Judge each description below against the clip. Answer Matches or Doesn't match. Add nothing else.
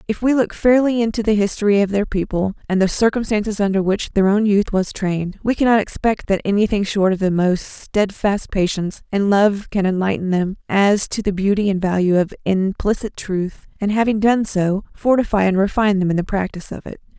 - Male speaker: Doesn't match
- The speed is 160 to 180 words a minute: Doesn't match